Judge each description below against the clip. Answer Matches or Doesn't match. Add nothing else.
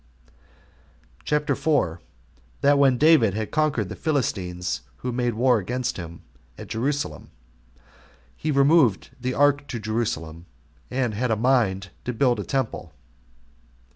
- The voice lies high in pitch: Doesn't match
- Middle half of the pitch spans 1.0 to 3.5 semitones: Doesn't match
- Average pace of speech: Doesn't match